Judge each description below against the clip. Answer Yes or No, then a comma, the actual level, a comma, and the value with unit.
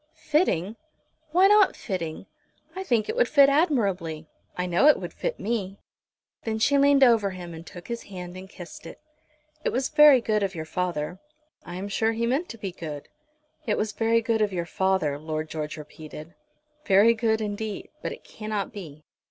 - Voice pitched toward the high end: Yes, high, 205 Hz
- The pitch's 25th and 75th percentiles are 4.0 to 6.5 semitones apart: Yes, average, 5.1 semitones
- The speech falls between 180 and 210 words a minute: Yes, average, 185 wpm